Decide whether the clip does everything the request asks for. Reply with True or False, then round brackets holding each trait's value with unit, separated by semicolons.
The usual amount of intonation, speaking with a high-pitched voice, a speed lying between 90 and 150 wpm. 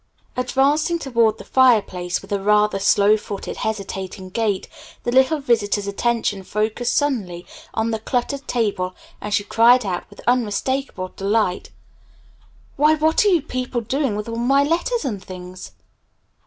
True (4.6 semitones; 225 Hz; 145 wpm)